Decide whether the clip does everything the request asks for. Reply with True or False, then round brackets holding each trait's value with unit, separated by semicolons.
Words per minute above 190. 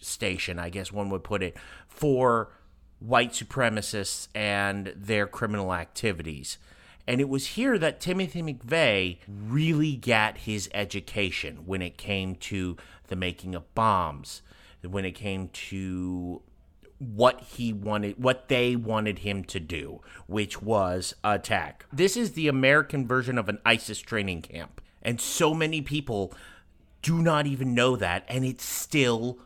False (145 wpm)